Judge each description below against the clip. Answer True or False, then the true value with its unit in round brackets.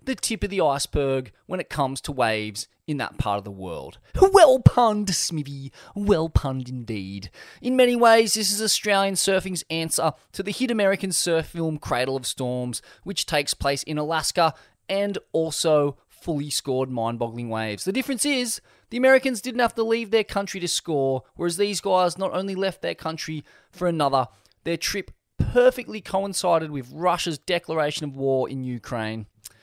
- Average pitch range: False (6.9 semitones)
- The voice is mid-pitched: True (160 Hz)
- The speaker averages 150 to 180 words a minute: True (170 wpm)